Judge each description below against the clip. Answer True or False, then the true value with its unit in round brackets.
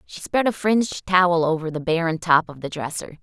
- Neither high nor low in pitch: True (170 Hz)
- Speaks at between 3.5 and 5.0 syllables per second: False (5.5 syllables/s)